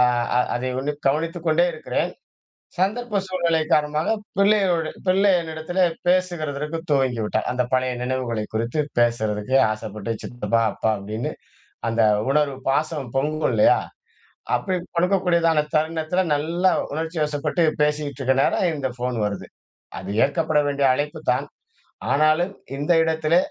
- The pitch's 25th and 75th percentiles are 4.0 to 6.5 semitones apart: Yes, average, 4.5 semitones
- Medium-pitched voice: Yes, medium, 150 Hz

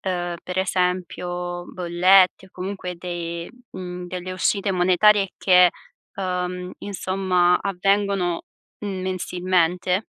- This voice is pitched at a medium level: Yes, medium, 180 Hz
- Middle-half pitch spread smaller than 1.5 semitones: Yes, narrow, 1.1 semitones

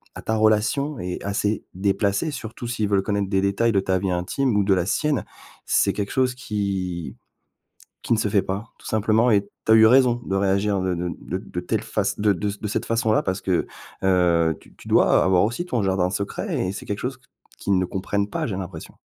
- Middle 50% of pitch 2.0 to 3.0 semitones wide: Yes, average, 2.7 semitones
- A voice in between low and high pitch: No, low, 100 Hz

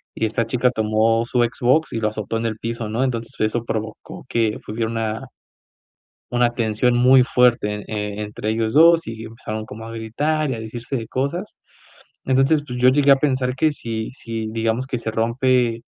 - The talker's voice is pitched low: Yes, low, 115 Hz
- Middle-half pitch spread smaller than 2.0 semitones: No, narrow, 2.5 semitones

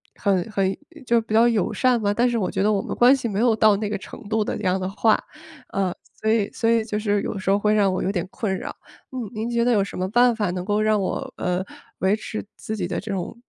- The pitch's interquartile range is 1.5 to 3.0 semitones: Yes, narrow, 2.6 semitones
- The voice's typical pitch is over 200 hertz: Yes, high, 210 Hz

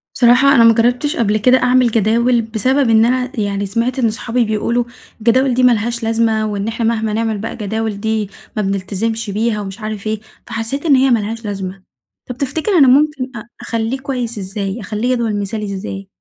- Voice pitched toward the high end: Yes, high, 225 Hz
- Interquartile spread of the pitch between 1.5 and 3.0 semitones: Yes, average, 2.7 semitones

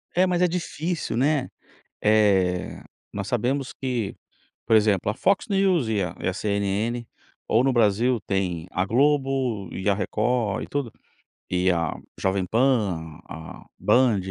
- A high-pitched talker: No, low, 110 Hz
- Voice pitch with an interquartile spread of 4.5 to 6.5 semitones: Yes, wide, 5.4 semitones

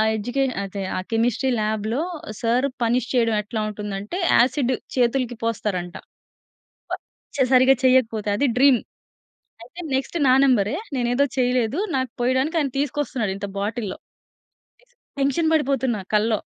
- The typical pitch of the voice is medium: No, high, 245 Hz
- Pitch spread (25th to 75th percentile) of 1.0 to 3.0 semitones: No, average, 3.6 semitones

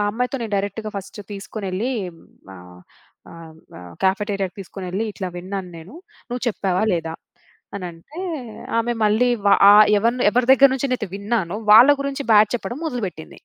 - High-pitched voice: Yes, high, 205 Hz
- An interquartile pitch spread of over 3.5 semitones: Yes, average, 4.3 semitones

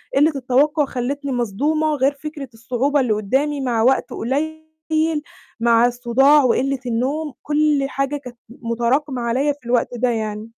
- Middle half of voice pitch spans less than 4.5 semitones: Yes, average, 3.4 semitones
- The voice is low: No, very high, 265 Hz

